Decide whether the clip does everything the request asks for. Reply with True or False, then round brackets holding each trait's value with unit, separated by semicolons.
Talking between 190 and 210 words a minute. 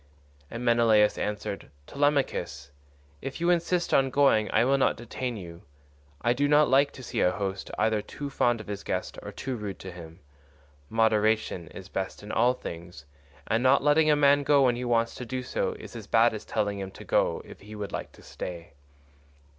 True (200 wpm)